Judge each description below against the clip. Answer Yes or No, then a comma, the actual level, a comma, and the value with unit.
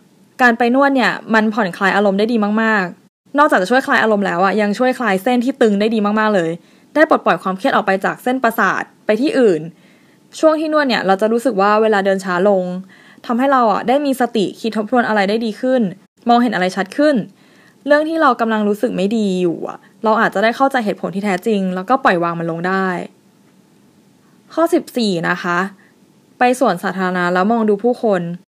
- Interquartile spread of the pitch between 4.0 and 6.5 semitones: Yes, average, 4.6 semitones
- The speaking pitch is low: No, high, 215 Hz